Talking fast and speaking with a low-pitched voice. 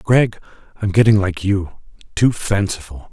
No: slow, 115 wpm; low, 100 Hz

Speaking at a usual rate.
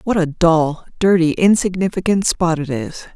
Yes: average, 150 wpm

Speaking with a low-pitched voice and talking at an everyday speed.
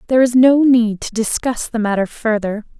No: high, 230 Hz; average, 195 wpm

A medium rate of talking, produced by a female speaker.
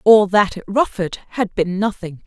Yes: average, 185 wpm; female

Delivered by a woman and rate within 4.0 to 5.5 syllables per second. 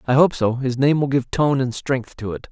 No: male; 5.2 syllables/s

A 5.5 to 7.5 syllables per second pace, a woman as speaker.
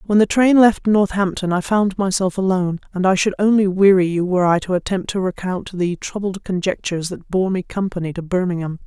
Yes: 5.6 syllables/s; female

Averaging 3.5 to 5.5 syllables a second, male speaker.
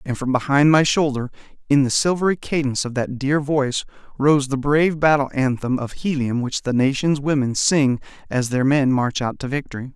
Yes: 5.3 syllables/s; male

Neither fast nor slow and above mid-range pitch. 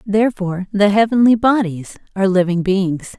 No: slow, 130 wpm; high, 200 Hz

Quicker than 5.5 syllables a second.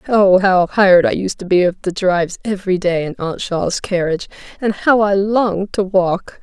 No: 5.0 syllables/s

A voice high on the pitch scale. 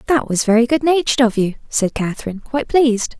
Yes: high, 240 Hz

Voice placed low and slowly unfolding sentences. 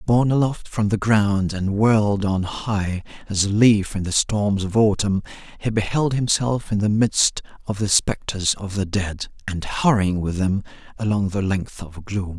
No: low, 100 Hz; average, 185 wpm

